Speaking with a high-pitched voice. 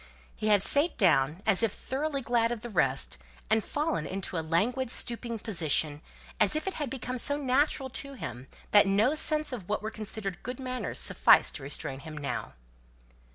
Yes: high, 220 Hz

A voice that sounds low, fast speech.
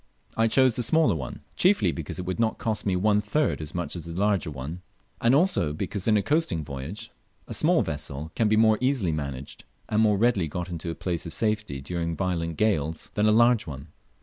Yes: very low, 95 Hz; fast, 215 wpm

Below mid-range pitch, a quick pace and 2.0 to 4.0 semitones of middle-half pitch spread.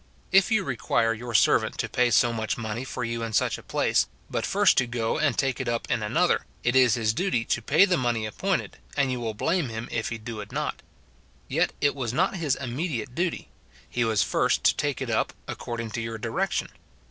Yes: low, 120 Hz; fast, 230 wpm; average, 3.6 semitones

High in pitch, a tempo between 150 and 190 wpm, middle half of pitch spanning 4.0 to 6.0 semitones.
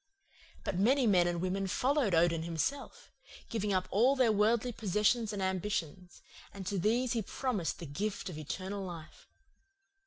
Yes: high, 200 Hz; average, 155 wpm; average, 4.4 semitones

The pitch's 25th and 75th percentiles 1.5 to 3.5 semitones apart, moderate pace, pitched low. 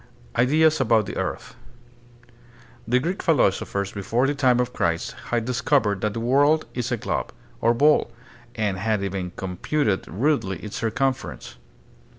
No: average, 5.2 semitones; average, 155 wpm; low, 120 Hz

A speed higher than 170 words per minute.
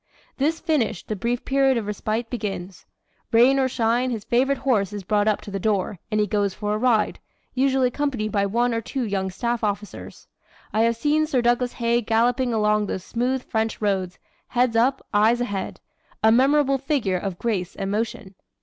Yes: average, 185 wpm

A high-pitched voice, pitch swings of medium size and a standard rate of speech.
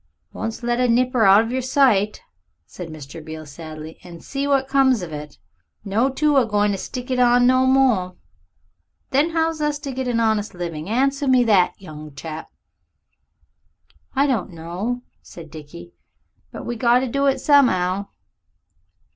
No: high, 230 Hz; wide, 6.9 semitones; average, 165 wpm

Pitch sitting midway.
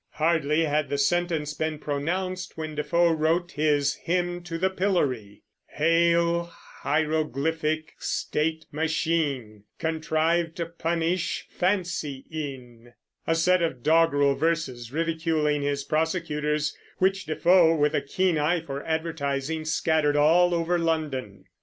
Yes: medium, 160 Hz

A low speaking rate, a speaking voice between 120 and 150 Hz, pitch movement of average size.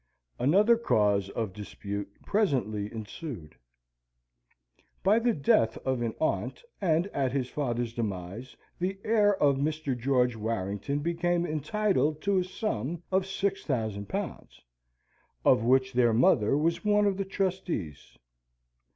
No: slow, 130 wpm; medium, 140 Hz; wide, 8.8 semitones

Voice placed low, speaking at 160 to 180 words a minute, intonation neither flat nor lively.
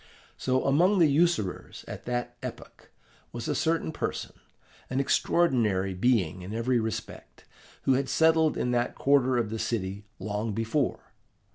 No: low, 120 Hz; average, 145 wpm; average, 4.6 semitones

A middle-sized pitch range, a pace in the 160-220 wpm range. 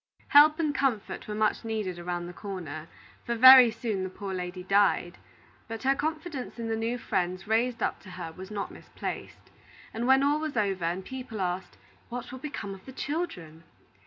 No: wide, 5.8 semitones; average, 190 wpm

